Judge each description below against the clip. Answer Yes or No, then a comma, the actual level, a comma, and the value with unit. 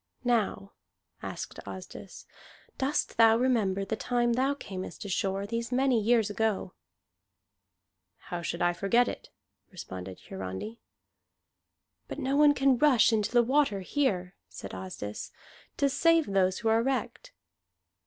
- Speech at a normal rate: No, slow, 130 wpm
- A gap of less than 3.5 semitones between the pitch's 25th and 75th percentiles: No, average, 5.2 semitones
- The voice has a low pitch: No, high, 225 Hz